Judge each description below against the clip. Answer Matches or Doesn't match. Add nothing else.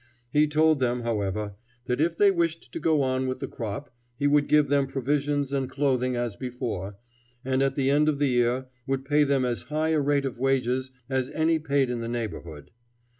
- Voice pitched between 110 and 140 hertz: Matches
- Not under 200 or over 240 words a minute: Matches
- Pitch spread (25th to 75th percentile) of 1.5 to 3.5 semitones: Matches